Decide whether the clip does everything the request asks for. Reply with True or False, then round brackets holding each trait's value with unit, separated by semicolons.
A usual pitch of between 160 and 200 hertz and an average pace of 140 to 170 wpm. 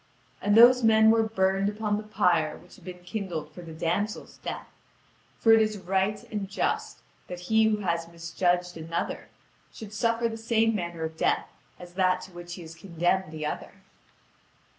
False (190 Hz; 180 wpm)